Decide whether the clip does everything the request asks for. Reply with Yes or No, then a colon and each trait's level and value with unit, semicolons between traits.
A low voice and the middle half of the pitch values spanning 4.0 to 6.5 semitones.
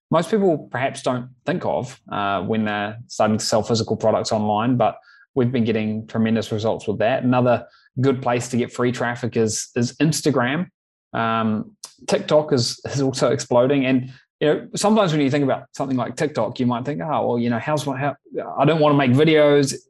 Yes: low, 125 Hz; average, 4.3 semitones